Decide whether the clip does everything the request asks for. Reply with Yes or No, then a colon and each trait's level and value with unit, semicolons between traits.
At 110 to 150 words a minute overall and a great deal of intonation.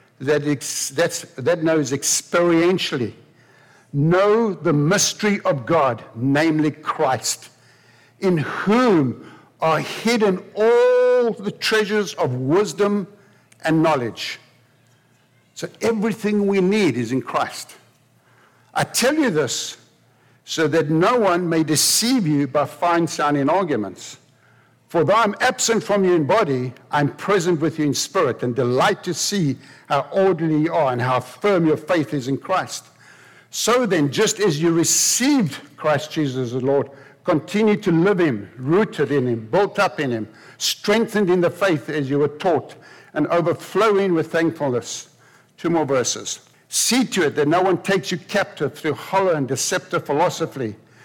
Yes: average, 145 wpm; wide, 6.0 semitones